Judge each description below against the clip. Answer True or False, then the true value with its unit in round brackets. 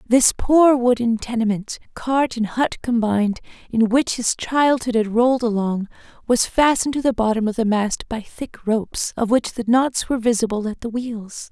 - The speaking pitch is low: False (235 Hz)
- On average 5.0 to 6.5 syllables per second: False (4.8 syllables/s)